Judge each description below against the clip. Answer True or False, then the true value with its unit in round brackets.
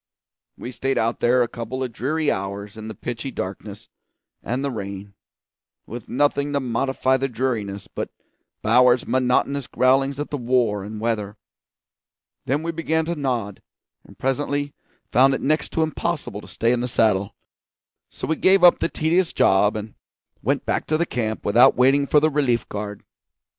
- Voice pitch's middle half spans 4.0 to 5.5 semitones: True (4.5 semitones)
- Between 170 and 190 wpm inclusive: True (175 wpm)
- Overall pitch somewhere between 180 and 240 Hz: False (125 Hz)